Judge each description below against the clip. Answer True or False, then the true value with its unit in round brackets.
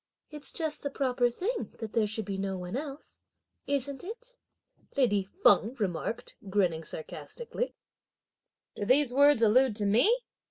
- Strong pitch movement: True (6.0 semitones)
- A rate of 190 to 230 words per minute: False (145 wpm)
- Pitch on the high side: True (245 Hz)